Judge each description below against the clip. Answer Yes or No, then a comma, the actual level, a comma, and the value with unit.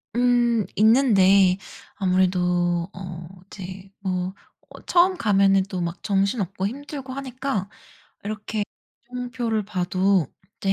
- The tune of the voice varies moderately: Yes, average, 4.5 semitones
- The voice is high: Yes, high, 195 Hz